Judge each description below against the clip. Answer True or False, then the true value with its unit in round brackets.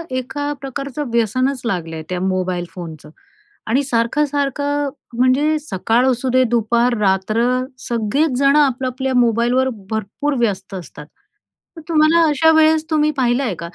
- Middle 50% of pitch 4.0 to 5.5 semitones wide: True (4.7 semitones)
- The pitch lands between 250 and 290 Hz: True (255 Hz)